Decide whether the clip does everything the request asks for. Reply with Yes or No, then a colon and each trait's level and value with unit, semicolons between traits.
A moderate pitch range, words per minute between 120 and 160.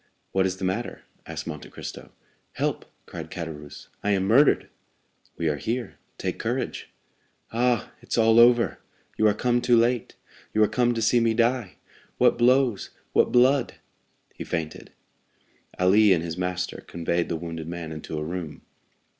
No: wide, 5.8 semitones; average, 155 wpm